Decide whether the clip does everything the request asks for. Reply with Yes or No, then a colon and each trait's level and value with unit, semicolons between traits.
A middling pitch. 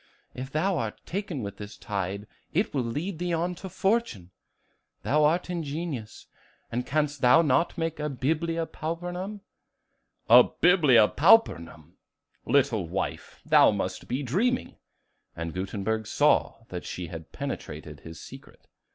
Yes: medium, 145 Hz